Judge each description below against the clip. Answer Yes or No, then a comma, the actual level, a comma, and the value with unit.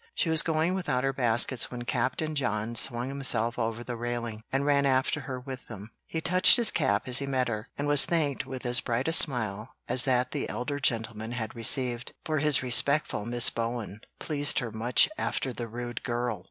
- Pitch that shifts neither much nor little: Yes, average, 3.1 semitones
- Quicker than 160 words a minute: Yes, average, 200 wpm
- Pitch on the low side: Yes, low, 125 Hz